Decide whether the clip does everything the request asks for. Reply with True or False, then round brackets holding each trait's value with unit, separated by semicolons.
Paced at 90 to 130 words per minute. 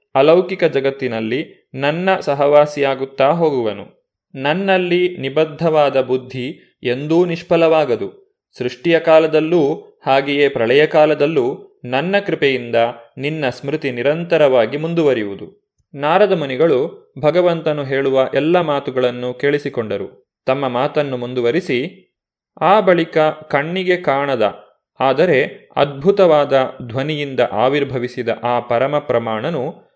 False (80 wpm)